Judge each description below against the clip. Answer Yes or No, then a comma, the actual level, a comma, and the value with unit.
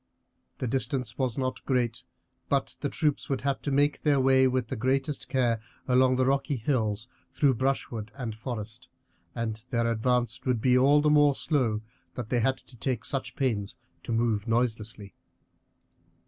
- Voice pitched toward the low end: Yes, low, 125 Hz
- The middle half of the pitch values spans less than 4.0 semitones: Yes, average, 2.8 semitones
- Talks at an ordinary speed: Yes, average, 165 wpm